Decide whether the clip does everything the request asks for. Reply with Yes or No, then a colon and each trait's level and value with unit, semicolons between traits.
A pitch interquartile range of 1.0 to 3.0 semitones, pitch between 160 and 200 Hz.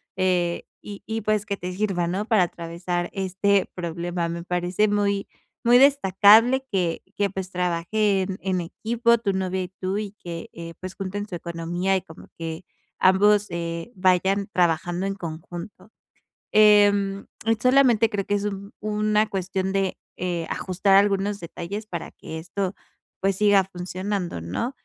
Yes: average, 2.7 semitones; high, 190 Hz